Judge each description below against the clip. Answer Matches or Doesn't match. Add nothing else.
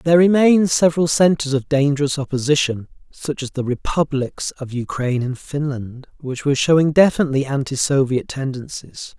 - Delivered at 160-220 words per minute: Doesn't match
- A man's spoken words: Matches